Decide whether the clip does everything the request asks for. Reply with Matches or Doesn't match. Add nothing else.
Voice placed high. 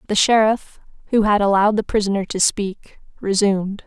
Matches